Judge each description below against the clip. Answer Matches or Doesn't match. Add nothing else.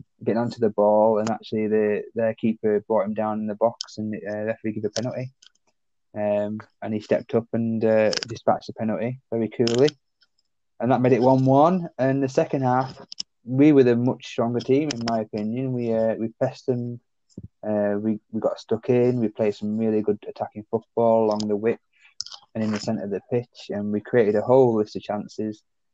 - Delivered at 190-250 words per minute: Matches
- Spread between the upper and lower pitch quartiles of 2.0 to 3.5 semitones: Matches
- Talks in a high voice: Doesn't match